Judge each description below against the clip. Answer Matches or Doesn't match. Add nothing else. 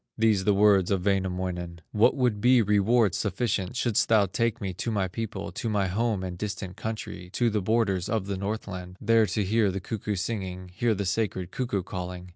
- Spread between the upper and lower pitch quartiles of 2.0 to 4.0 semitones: Matches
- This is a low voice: Matches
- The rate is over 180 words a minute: Matches